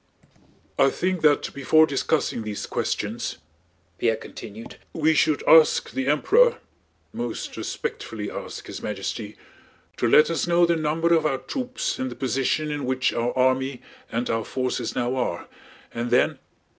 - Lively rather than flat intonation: No, average, 4.3 semitones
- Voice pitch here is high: No, low, 135 Hz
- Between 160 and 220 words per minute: No, average, 145 wpm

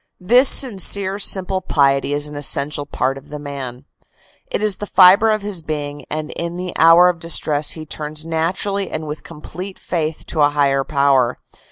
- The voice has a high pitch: No, medium, 155 Hz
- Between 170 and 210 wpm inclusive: Yes, average, 180 wpm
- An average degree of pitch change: Yes, average, 4.2 semitones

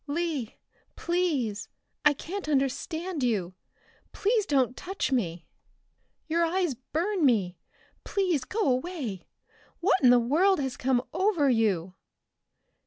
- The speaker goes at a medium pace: No, slow, 115 wpm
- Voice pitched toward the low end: No, very high, 285 Hz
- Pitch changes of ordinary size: No, wide, 6.6 semitones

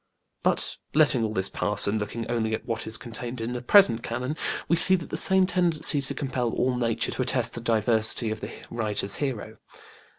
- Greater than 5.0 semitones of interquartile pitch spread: No, average, 3.8 semitones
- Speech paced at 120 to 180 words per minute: No, average, 195 wpm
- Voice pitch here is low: Yes, low, 120 Hz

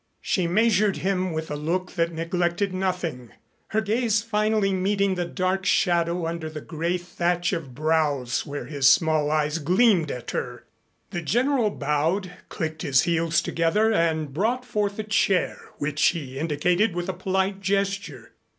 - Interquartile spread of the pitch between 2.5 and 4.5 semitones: Yes, average, 3.9 semitones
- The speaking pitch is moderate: Yes, medium, 175 Hz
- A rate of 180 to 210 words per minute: No, average, 155 wpm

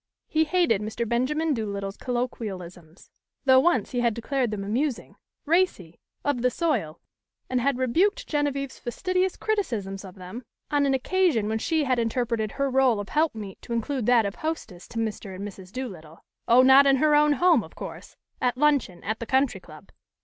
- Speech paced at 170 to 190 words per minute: Yes, average, 180 wpm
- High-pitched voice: Yes, very high, 250 Hz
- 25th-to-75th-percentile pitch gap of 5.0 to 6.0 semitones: Yes, wide, 5.5 semitones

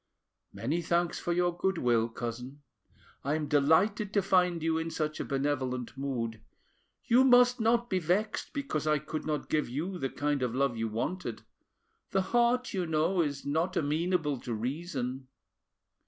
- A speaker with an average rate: Yes, average, 160 wpm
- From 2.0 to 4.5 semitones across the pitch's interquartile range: No, average, 5.2 semitones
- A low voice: No, medium, 155 Hz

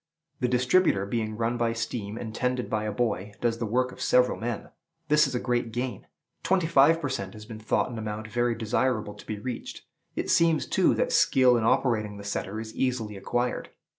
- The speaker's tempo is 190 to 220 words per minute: Yes, fast, 205 wpm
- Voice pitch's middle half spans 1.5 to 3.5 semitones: Yes, average, 2.7 semitones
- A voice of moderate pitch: No, low, 115 Hz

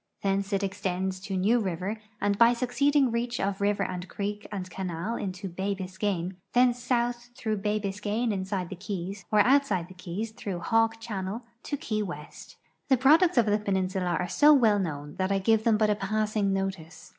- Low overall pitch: No, high, 200 Hz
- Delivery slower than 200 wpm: Yes, average, 190 wpm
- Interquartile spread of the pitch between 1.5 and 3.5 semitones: Yes, average, 3.2 semitones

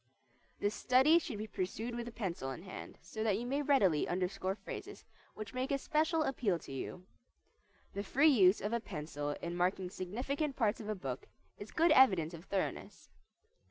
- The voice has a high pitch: Yes, high, 210 Hz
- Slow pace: No, average, 180 wpm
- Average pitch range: No, wide, 6.1 semitones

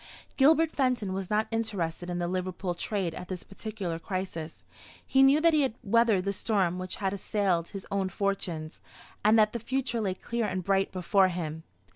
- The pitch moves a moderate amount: Yes, average, 3.8 semitones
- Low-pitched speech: No, high, 195 Hz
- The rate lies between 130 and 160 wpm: No, average, 185 wpm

